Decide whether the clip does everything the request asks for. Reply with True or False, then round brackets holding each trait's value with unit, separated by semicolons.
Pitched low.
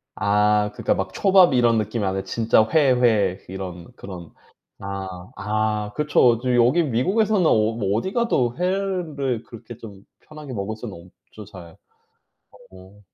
True (110 Hz)